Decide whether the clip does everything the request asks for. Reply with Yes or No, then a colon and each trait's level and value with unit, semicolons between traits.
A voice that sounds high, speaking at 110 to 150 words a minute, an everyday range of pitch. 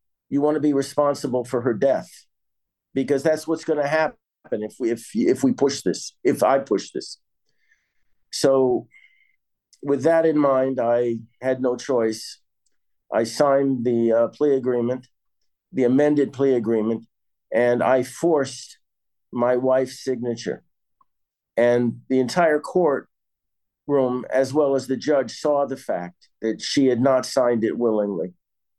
No: low, 130 Hz; average, 145 wpm; average, 3.1 semitones